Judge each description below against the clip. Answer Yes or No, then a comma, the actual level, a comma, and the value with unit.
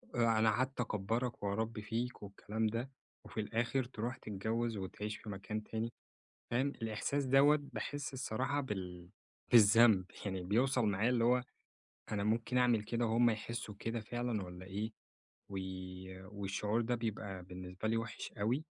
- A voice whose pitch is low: Yes, low, 115 Hz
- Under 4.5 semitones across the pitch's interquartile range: Yes, average, 2.8 semitones